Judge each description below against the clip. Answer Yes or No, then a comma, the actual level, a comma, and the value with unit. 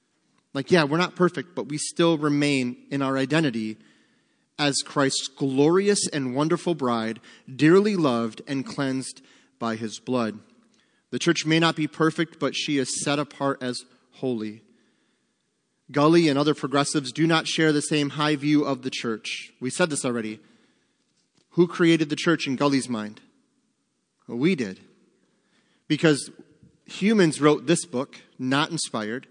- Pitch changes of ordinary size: Yes, average, 3.8 semitones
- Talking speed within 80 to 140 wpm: No, average, 150 wpm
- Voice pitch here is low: No, medium, 145 Hz